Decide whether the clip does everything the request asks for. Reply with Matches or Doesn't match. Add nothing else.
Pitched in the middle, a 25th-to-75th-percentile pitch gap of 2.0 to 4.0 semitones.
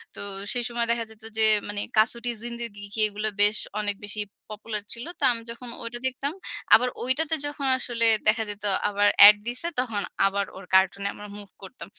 Doesn't match